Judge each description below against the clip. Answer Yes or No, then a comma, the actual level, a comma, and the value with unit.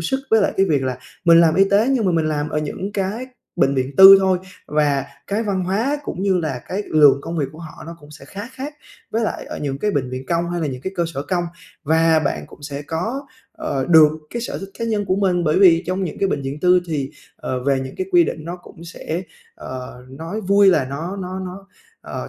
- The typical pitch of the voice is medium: Yes, medium, 170 Hz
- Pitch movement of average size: Yes, average, 4.9 semitones